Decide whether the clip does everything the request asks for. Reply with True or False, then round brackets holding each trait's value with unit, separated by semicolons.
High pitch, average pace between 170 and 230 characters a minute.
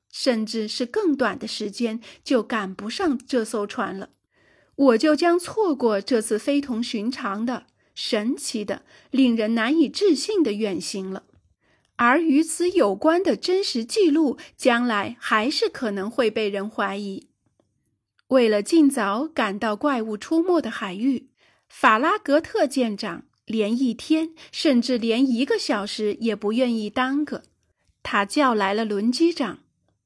True (245 Hz; 210 characters per minute)